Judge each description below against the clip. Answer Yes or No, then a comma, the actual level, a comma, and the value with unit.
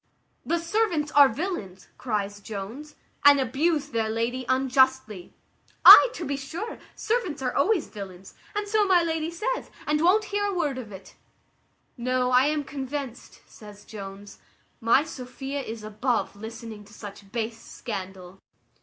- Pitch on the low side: No, very high, 260 Hz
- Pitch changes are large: Yes, wide, 6.5 semitones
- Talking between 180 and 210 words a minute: No, average, 145 wpm